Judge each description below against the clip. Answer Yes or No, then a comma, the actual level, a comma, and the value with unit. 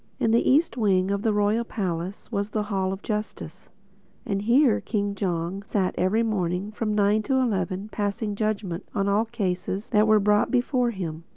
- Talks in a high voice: Yes, high, 205 Hz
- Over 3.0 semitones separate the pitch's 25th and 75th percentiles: No, narrow, 2.4 semitones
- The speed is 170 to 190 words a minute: Yes, average, 180 wpm